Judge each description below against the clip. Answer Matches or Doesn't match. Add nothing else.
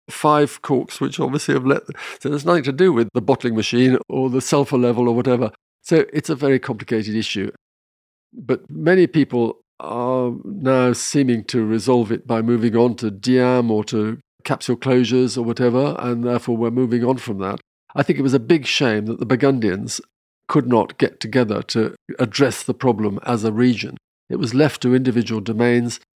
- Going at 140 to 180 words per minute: Doesn't match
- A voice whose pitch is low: Matches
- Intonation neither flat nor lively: Doesn't match